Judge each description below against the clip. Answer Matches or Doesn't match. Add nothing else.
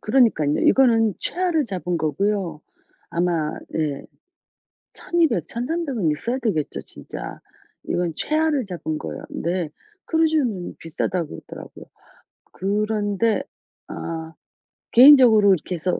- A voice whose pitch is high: Matches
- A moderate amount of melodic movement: Doesn't match